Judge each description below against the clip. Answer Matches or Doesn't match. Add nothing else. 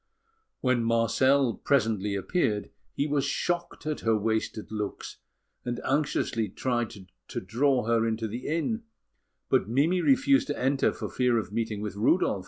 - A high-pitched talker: Doesn't match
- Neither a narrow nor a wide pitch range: Matches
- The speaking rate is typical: Matches